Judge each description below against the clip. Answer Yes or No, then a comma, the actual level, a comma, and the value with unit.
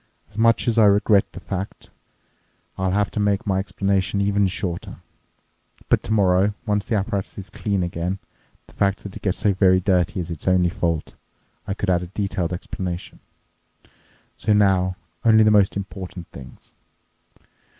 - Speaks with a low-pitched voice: Yes, very low, 95 Hz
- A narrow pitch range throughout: Yes, narrow, 2.0 semitones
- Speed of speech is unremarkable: Yes, average, 155 wpm